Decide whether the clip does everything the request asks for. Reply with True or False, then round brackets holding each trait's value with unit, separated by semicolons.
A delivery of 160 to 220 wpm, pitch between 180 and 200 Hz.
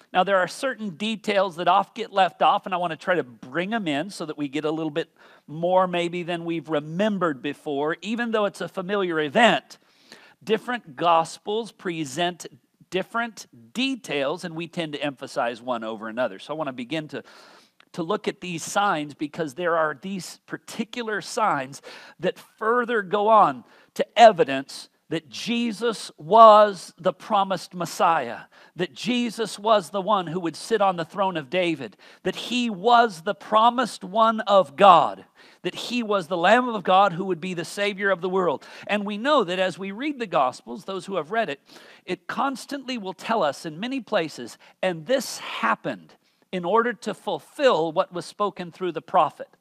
True (185 wpm; 190 Hz)